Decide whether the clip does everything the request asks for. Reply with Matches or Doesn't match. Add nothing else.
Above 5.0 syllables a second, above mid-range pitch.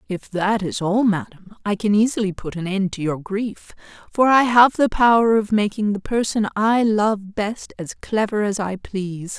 Doesn't match